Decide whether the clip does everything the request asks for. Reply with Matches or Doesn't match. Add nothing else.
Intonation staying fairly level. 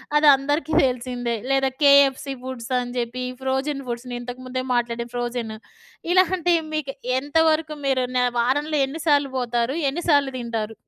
Doesn't match